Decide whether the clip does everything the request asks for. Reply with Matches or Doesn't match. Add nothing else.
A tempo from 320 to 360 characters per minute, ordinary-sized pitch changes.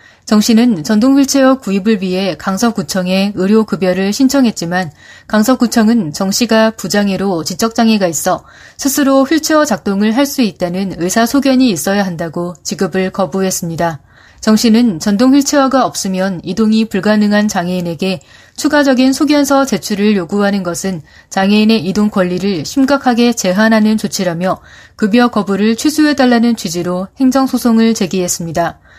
Matches